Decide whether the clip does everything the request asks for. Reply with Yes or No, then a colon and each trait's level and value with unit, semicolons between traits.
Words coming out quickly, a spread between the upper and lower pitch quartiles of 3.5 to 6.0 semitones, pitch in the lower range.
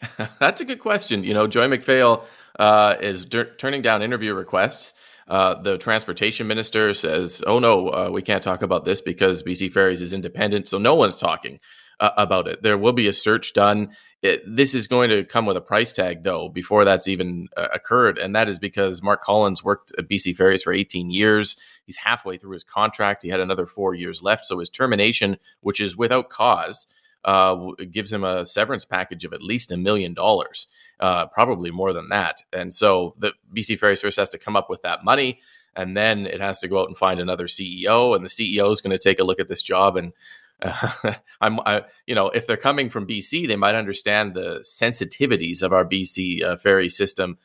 No: fast, 215 wpm; narrow, 2.4 semitones; low, 100 Hz